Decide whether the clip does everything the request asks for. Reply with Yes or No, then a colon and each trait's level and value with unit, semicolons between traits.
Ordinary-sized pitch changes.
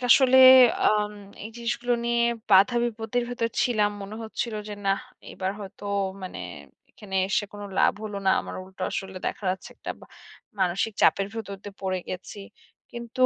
Yes: average, 3.3 semitones